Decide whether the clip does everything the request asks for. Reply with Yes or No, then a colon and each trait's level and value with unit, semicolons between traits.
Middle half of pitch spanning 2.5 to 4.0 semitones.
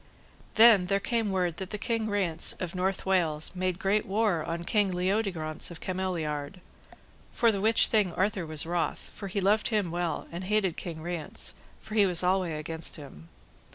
Yes: average, 3.4 semitones